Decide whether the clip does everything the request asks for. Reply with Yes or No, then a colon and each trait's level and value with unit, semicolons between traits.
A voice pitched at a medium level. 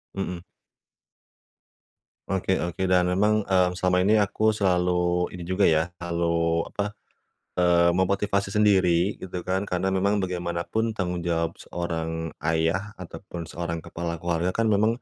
No: very low, 90 Hz